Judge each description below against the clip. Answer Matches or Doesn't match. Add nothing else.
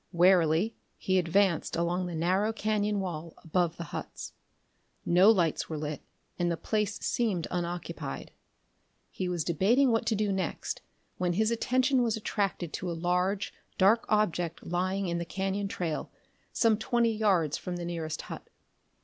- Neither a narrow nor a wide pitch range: Matches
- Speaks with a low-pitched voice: Doesn't match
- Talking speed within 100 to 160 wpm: Matches